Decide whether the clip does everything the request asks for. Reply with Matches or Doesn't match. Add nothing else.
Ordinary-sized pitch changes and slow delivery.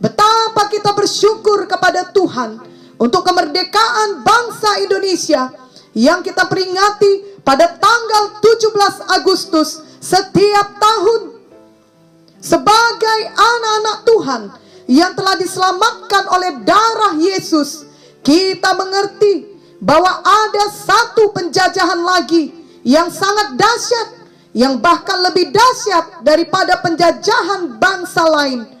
Matches